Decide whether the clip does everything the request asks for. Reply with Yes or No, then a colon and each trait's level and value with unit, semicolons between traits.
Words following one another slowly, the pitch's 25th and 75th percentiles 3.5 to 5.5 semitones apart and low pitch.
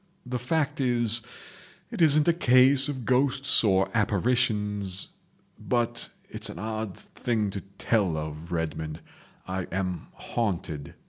Yes: slow, 105 wpm; average, 5.1 semitones; low, 110 Hz